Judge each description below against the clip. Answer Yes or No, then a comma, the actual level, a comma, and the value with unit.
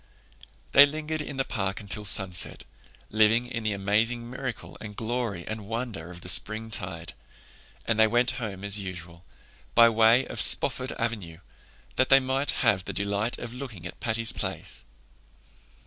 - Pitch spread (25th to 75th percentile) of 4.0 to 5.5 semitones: No, average, 3.6 semitones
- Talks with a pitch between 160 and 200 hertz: No, low, 110 Hz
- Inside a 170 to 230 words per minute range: No, average, 155 wpm